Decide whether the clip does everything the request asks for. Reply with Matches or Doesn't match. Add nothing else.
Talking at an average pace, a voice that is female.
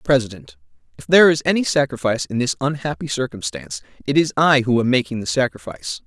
Doesn't match